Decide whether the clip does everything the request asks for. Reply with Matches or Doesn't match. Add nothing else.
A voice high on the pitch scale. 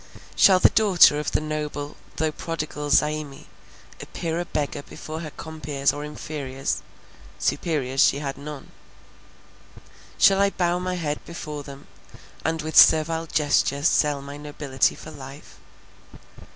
Doesn't match